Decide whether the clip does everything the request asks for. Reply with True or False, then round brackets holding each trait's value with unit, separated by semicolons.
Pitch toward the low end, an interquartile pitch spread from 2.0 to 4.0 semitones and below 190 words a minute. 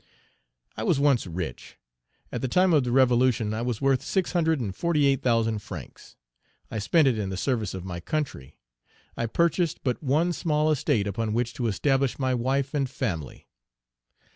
False (130 Hz; 4.9 semitones; 180 wpm)